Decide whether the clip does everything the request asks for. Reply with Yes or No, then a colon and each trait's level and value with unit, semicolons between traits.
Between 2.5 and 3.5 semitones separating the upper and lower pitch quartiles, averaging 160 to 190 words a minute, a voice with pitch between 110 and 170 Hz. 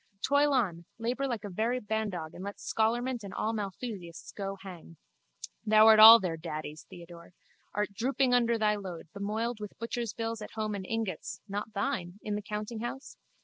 No: average, 3.2 semitones; average, 175 wpm; high, 210 Hz